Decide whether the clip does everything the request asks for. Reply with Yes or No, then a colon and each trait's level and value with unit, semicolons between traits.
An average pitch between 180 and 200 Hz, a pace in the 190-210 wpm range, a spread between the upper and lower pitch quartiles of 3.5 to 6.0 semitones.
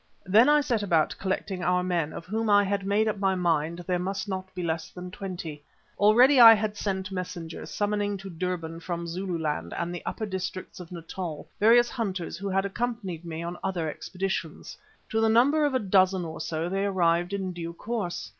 No: medium, 185 Hz; average, 195 wpm; average, 3.1 semitones